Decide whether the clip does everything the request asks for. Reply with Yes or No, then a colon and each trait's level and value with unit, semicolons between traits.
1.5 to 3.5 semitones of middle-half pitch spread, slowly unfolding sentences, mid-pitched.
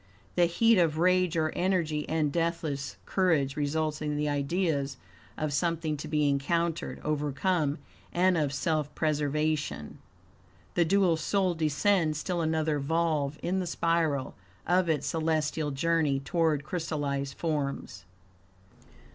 Yes: narrow, 2.6 semitones; slow, 125 wpm; medium, 155 Hz